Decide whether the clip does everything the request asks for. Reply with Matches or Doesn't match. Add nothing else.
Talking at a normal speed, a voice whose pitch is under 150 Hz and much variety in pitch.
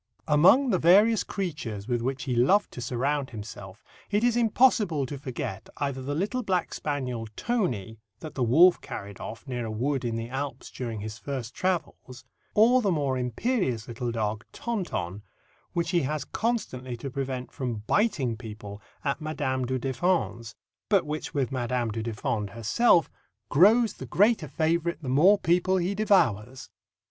Matches